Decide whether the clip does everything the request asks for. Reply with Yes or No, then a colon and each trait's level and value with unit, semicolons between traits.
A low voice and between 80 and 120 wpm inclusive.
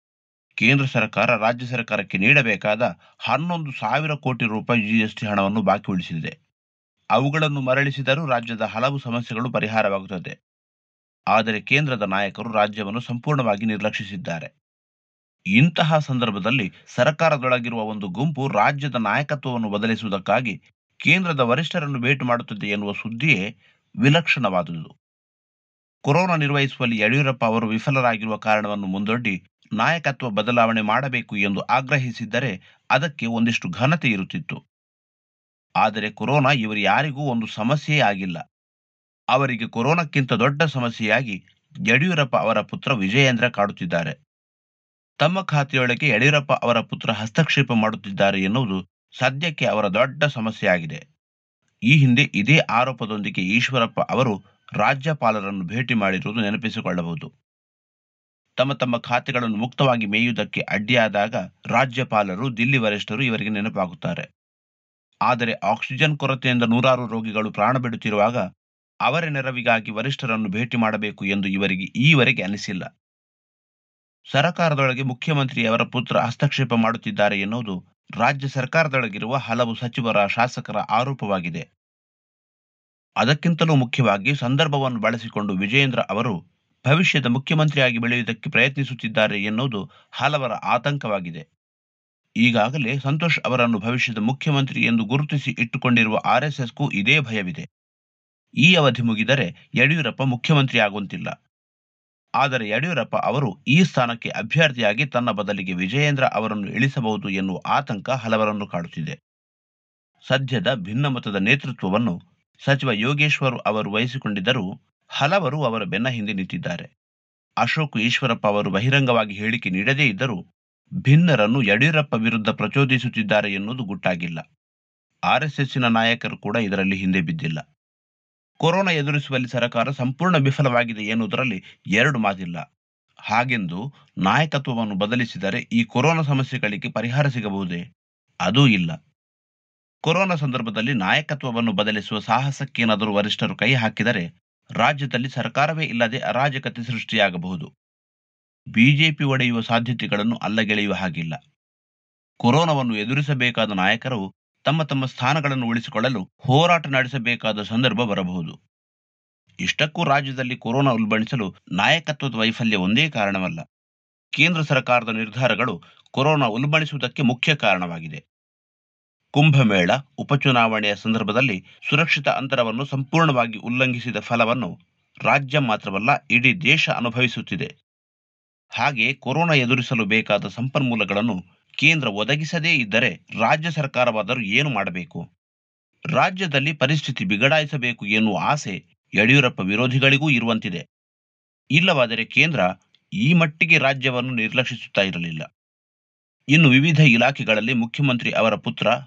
Yes: low, 120 Hz; average, 95 wpm